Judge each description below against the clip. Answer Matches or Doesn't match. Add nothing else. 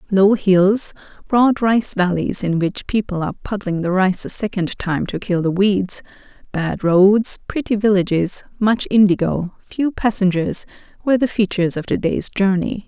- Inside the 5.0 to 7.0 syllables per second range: Doesn't match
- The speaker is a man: Doesn't match